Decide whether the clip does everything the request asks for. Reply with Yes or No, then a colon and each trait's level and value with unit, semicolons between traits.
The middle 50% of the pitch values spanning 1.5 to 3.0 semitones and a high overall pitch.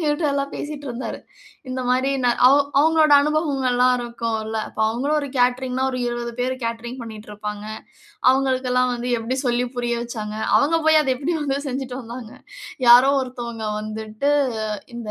Yes: average, 2.7 semitones; very high, 250 Hz